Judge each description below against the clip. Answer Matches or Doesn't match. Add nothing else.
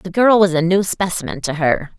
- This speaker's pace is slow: Doesn't match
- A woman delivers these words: Matches